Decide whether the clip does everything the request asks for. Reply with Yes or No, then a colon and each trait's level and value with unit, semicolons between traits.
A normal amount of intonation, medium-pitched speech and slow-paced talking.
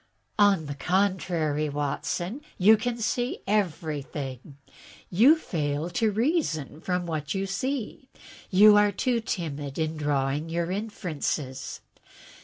No: wide, 5.9 semitones; medium, 175 Hz; slow, 115 wpm